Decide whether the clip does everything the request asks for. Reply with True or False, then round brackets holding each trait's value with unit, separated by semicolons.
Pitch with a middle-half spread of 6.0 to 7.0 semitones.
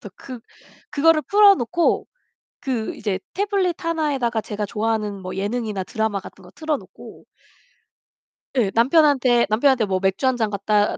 True (6.3 semitones)